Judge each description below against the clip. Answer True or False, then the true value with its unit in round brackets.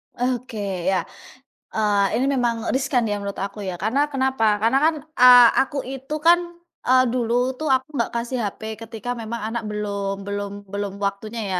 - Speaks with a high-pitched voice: True (230 Hz)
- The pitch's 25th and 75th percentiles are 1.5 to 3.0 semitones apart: False (4.2 semitones)